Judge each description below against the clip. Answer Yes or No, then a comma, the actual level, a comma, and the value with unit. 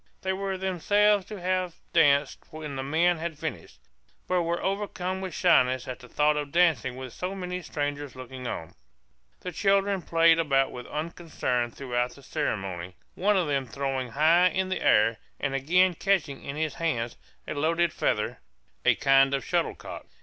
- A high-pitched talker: No, medium, 155 Hz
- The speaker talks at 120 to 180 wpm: Yes, average, 170 wpm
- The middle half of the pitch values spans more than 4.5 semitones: Yes, average, 5.2 semitones